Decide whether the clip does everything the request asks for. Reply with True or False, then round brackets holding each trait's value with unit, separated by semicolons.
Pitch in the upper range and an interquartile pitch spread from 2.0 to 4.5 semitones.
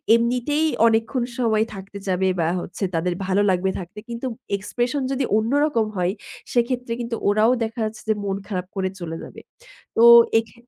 True (220 Hz; 3.9 semitones)